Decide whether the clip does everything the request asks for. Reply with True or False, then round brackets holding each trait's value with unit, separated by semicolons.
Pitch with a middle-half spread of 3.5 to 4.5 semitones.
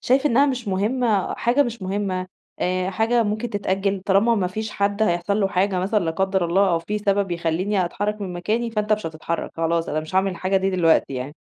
False (2.8 semitones)